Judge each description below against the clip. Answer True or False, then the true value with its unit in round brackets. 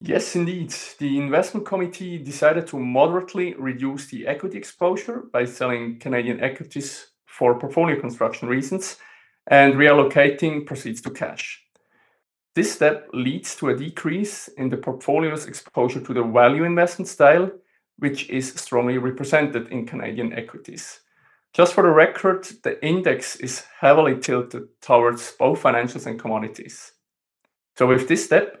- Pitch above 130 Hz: True (140 Hz)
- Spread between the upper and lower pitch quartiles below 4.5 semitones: False (5.3 semitones)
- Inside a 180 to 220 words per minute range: False (135 wpm)